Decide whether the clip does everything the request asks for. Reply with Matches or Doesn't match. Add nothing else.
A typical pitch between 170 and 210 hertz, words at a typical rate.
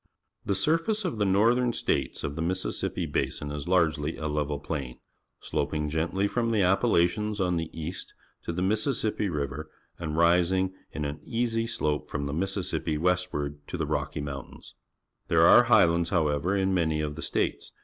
Doesn't match